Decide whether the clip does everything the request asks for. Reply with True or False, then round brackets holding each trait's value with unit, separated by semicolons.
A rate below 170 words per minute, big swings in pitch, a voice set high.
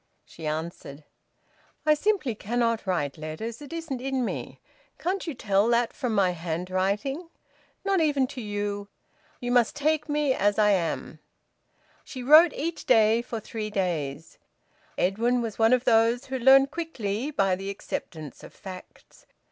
True (150 wpm; 5.8 semitones; 230 Hz)